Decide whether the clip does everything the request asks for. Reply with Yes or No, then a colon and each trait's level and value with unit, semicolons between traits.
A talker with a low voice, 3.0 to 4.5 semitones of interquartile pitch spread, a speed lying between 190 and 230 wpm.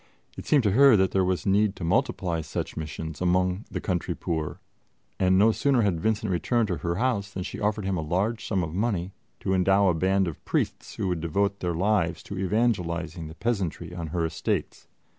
Yes: very low, 95 Hz; average, 3.4 semitones; fast, 205 wpm